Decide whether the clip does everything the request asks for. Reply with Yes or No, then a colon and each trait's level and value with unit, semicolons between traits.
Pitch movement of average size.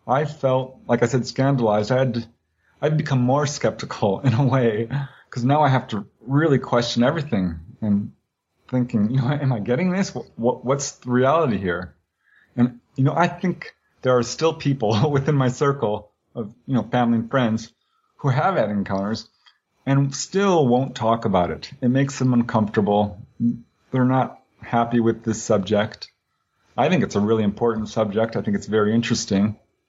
Yes: average, 3.7 semitones